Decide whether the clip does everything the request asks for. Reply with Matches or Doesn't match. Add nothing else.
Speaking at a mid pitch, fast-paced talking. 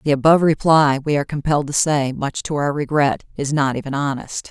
Matches